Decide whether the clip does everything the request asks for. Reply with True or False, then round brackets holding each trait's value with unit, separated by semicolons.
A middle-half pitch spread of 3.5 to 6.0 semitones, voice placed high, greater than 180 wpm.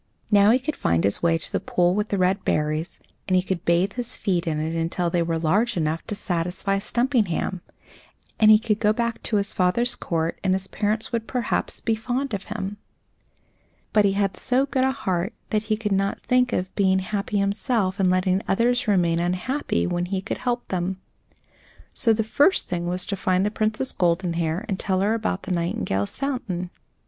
True (3.8 semitones; 195 Hz; 200 wpm)